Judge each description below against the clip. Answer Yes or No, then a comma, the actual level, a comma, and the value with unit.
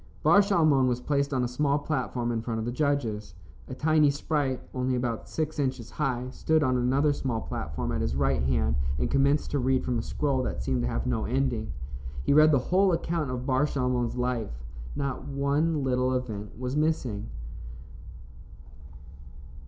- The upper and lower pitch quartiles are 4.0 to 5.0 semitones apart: No, average, 3.4 semitones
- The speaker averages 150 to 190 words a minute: Yes, average, 175 wpm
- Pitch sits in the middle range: No, low, 130 Hz